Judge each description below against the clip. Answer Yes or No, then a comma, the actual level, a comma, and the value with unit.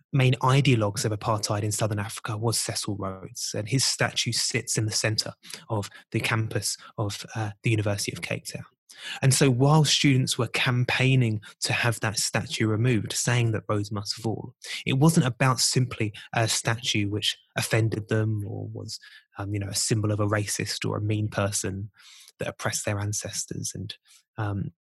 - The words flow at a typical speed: Yes, average, 175 wpm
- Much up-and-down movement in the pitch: No, average, 3.1 semitones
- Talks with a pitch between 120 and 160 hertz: No, low, 110 Hz